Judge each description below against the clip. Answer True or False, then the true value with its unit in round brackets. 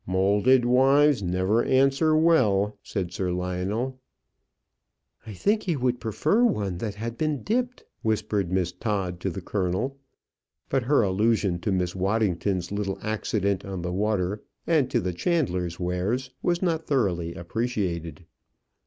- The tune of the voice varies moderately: False (6.0 semitones)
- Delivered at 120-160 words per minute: True (140 wpm)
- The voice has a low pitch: True (105 Hz)